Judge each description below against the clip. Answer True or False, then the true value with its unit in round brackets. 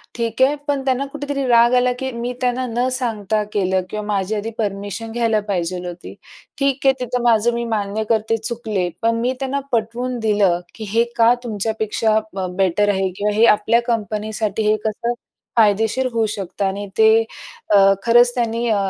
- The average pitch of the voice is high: True (225 Hz)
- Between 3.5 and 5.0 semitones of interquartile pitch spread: False (2.7 semitones)